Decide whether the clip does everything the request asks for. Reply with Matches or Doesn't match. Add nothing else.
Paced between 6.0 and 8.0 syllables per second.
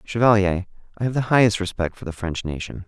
Matches